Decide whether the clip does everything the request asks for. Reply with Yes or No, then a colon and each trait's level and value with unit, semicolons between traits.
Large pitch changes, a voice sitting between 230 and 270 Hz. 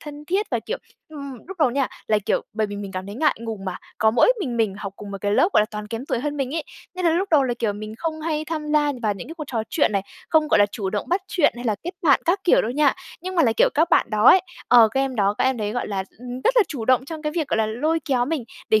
Yes: wide, 6.5 semitones; very high, 260 Hz